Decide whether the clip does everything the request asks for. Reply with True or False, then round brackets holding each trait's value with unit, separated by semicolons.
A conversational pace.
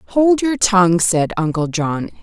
True (160 wpm)